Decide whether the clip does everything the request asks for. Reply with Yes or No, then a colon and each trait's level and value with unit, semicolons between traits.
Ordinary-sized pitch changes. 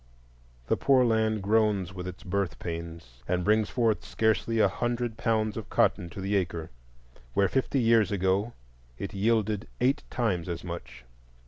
Yes: average, 3.8 semitones